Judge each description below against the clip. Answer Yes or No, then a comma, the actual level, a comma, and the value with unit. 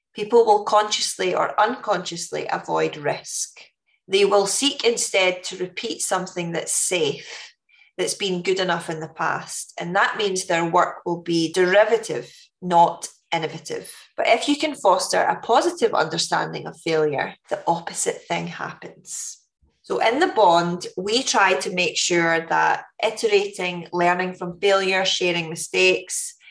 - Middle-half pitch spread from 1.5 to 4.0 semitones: No, average, 5.3 semitones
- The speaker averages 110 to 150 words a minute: Yes, average, 145 wpm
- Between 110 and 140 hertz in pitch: No, high, 190 Hz